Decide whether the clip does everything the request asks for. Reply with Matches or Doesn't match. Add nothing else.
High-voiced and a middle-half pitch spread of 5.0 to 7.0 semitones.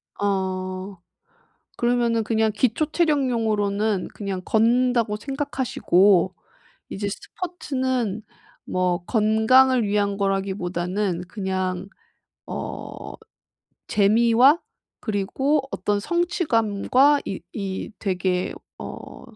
Doesn't match